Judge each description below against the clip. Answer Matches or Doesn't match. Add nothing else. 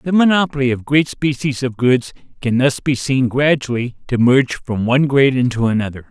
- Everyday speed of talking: Matches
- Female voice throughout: Doesn't match